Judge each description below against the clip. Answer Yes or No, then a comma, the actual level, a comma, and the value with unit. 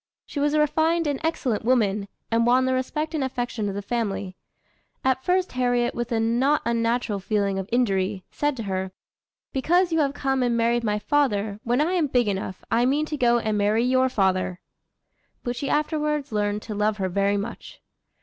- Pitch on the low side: No, high, 240 Hz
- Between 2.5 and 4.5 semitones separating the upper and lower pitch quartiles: No, average, 5.0 semitones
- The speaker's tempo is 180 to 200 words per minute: Yes, average, 195 wpm